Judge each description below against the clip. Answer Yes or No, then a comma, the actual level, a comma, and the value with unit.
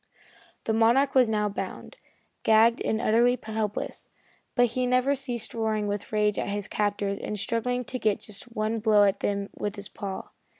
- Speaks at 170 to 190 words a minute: Yes, average, 175 wpm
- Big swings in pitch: No, narrow, 2.6 semitones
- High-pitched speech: Yes, high, 220 Hz